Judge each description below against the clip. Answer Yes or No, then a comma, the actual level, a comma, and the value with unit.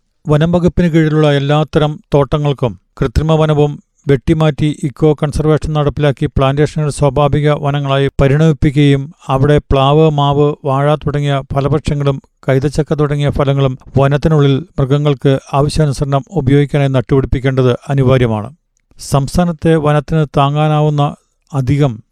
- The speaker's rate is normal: Yes, average, 90 wpm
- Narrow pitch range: Yes, narrow, 1.8 semitones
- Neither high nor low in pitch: Yes, medium, 145 Hz